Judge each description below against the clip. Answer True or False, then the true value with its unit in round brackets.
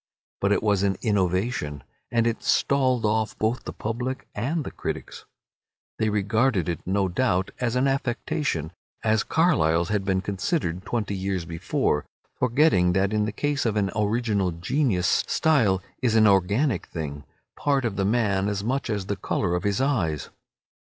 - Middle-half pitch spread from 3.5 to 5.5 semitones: True (4.6 semitones)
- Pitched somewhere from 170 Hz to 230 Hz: False (105 Hz)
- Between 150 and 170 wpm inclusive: True (165 wpm)